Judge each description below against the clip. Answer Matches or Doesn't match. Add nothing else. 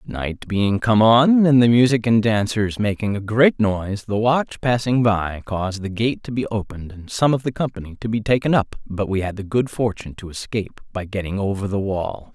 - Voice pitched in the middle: Doesn't match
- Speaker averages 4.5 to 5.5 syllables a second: Matches